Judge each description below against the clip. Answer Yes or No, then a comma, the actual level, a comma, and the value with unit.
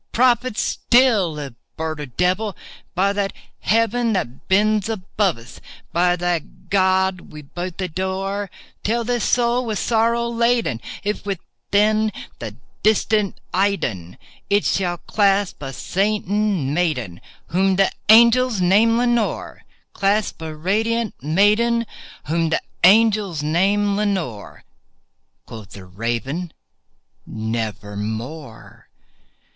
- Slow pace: Yes, slow, 120 wpm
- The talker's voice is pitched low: No, high, 195 Hz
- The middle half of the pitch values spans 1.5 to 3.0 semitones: No, wide, 5.4 semitones